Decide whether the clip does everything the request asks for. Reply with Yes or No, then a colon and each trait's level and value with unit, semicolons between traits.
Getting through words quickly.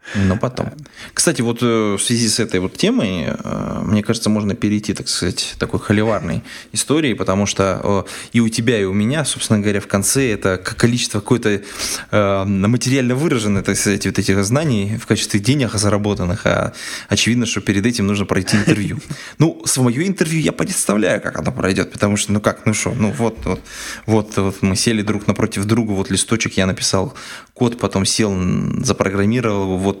Yes: fast, 170 wpm